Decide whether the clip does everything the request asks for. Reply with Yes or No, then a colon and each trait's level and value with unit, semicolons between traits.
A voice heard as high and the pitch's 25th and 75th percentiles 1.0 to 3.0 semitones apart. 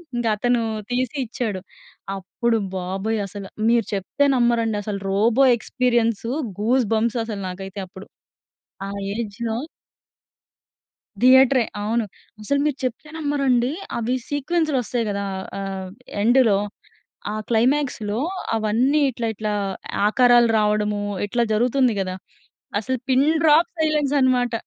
No: high, 235 Hz; average, 3.5 semitones